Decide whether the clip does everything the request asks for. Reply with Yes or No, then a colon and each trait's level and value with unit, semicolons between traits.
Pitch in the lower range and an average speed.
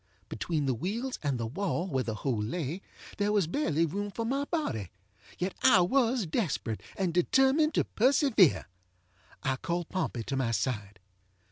No: medium, 175 Hz; average, 155 wpm